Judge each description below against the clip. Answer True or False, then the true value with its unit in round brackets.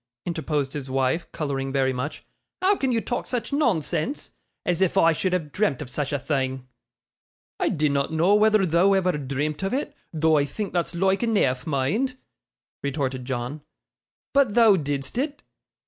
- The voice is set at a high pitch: False (160 Hz)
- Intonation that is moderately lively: False (6.8 semitones)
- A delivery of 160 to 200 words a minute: True (170 wpm)